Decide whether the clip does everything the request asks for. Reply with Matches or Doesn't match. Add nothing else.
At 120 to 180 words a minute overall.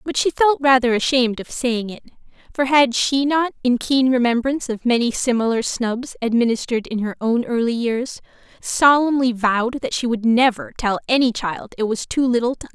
Doesn't match